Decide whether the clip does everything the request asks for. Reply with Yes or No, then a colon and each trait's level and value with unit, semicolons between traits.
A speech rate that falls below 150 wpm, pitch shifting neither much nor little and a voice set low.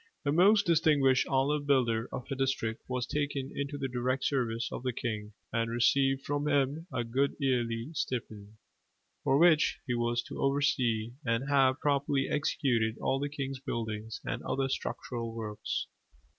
No: average, 155 wpm; average, 3.4 semitones; low, 130 Hz